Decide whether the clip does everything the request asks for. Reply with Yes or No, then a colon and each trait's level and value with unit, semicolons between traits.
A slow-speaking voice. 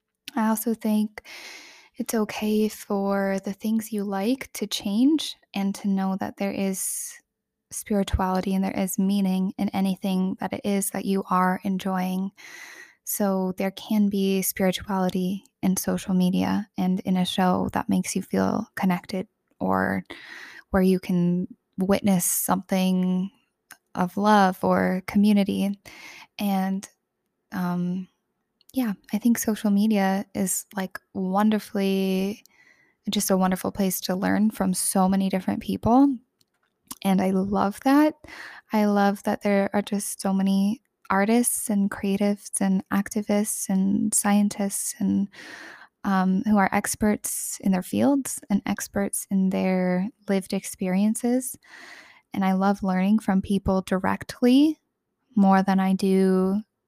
Yes: slow, 130 wpm